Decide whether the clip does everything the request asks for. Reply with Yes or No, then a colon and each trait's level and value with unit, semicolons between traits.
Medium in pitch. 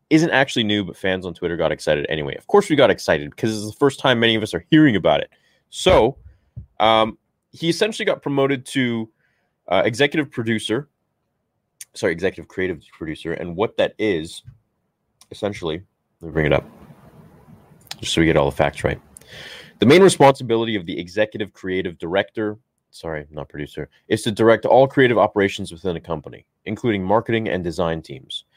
No: low, 110 Hz